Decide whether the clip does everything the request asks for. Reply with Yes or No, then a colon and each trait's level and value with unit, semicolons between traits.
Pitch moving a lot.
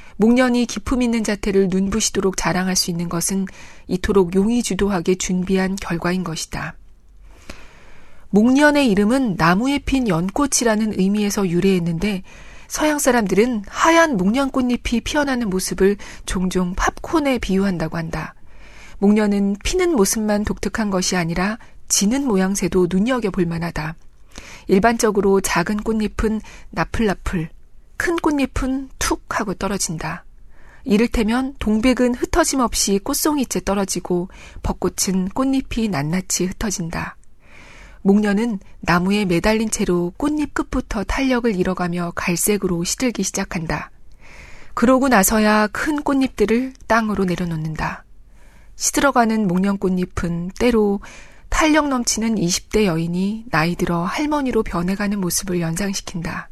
No: average, 4.5 semitones